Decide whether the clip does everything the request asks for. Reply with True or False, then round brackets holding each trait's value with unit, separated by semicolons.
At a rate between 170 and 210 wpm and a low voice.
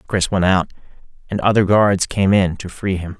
True (205 wpm; 95 Hz)